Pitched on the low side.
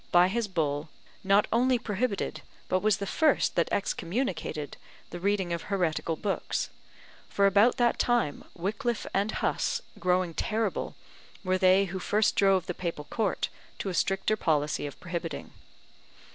No: high, 195 Hz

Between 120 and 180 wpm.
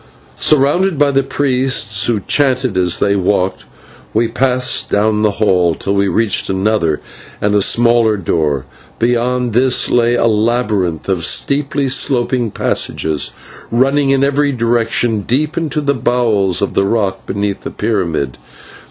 Yes: average, 145 wpm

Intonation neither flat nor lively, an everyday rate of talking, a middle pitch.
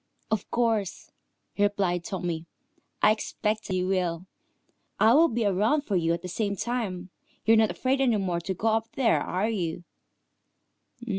No: average, 3.7 semitones; average, 155 wpm; high, 205 Hz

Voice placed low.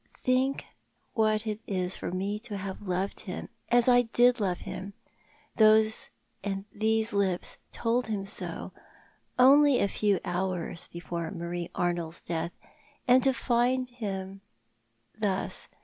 No: high, 205 Hz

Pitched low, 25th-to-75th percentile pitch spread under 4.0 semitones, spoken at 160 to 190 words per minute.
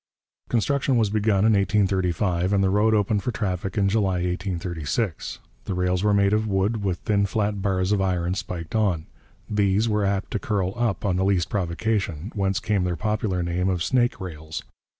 Yes: low, 100 Hz; narrow, 2.6 semitones; average, 180 wpm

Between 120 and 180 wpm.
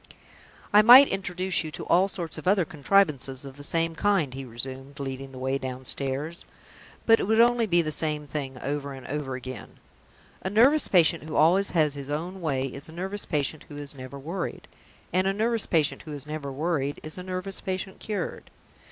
No: average, 195 wpm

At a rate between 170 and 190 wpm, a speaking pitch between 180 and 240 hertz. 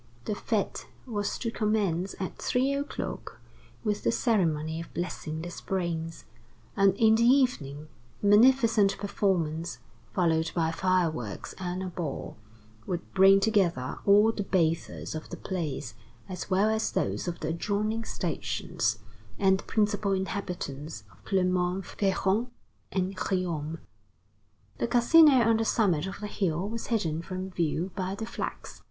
No: average, 145 wpm; high, 190 Hz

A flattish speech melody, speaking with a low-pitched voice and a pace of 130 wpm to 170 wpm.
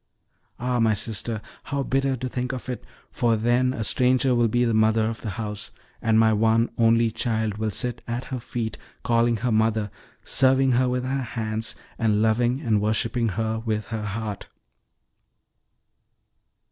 Yes: narrow, 2.1 semitones; low, 115 Hz; average, 165 wpm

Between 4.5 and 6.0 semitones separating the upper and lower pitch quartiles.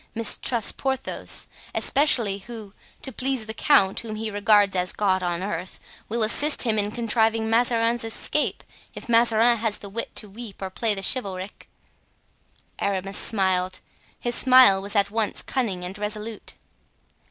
No: average, 2.9 semitones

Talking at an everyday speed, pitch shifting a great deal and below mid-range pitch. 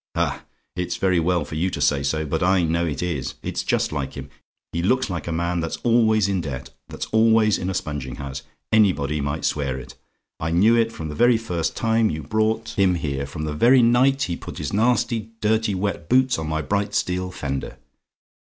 No: fast, 210 wpm; wide, 6.3 semitones; very low, 90 Hz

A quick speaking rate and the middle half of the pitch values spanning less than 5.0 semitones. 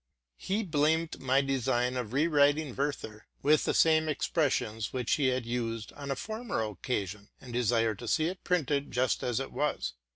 No: average, 185 wpm; average, 4.4 semitones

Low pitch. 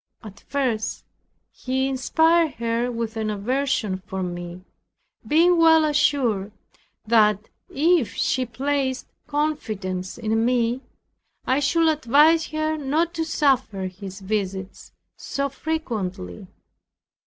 No: very high, 255 Hz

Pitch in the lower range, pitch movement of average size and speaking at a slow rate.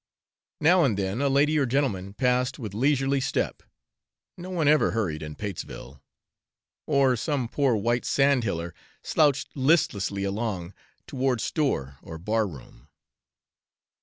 No: low, 125 Hz; wide, 6.0 semitones; slow, 130 wpm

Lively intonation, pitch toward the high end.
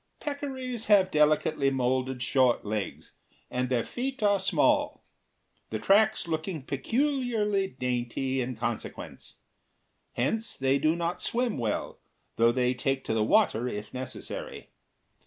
No: wide, 8.7 semitones; medium, 140 Hz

